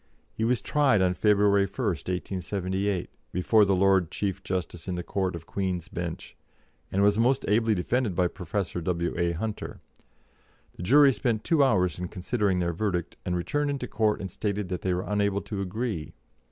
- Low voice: Yes, very low, 95 Hz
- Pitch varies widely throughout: No, average, 3.1 semitones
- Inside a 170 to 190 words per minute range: Yes, average, 175 wpm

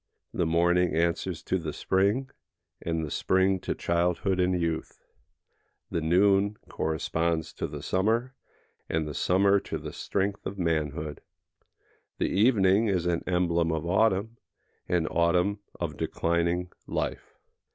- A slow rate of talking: Yes, slow, 130 wpm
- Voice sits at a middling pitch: No, very low, 90 Hz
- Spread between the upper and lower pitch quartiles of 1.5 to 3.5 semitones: Yes, average, 2.7 semitones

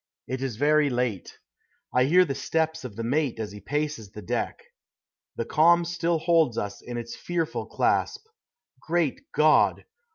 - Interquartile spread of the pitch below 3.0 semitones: No, average, 5.3 semitones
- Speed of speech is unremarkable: Yes, average, 160 wpm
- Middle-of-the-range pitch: Yes, medium, 145 Hz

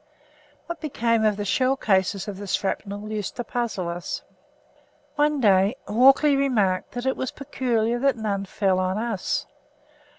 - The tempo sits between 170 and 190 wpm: No, average, 155 wpm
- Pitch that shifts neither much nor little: Yes, average, 4.9 semitones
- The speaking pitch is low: No, high, 220 Hz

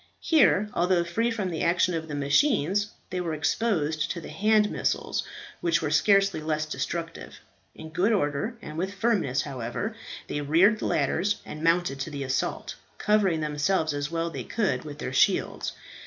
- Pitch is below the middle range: No, medium, 170 Hz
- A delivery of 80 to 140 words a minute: No, average, 175 wpm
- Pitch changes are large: No, average, 5.0 semitones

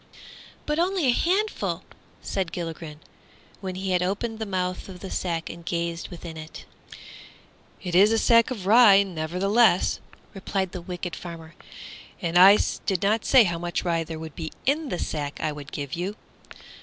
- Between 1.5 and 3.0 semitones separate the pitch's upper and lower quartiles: No, average, 3.7 semitones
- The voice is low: No, medium, 180 Hz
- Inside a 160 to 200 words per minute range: Yes, average, 170 wpm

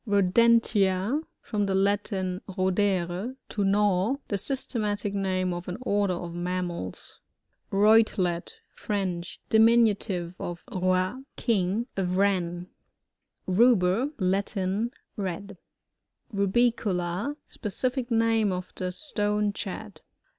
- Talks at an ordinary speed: No, slow, 110 wpm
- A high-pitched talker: Yes, high, 195 Hz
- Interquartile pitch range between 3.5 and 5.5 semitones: No, average, 3.0 semitones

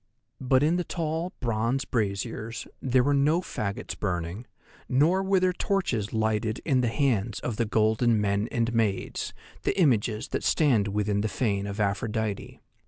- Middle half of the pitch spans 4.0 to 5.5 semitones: Yes, average, 4.8 semitones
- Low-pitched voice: Yes, low, 115 Hz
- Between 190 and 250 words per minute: No, average, 160 wpm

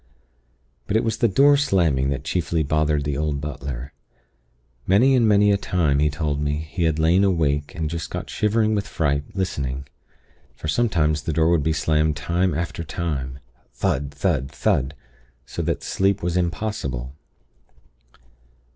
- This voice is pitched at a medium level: No, very low, 80 Hz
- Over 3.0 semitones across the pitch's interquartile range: Yes, average, 4.5 semitones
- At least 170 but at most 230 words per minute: No, average, 155 wpm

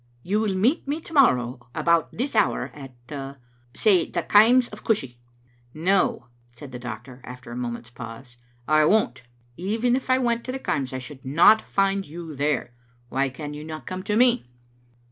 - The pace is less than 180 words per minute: No, average, 185 wpm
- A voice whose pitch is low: No, medium, 155 Hz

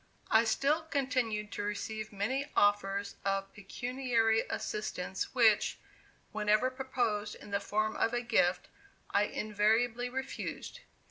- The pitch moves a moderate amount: Yes, average, 3.2 semitones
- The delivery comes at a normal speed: No, slow, 120 wpm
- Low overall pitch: No, high, 220 Hz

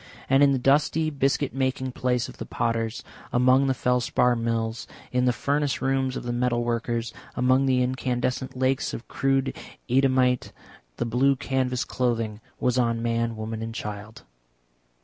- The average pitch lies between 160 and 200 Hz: No, low, 125 Hz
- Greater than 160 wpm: No, average, 155 wpm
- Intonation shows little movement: Yes, narrow, 2.1 semitones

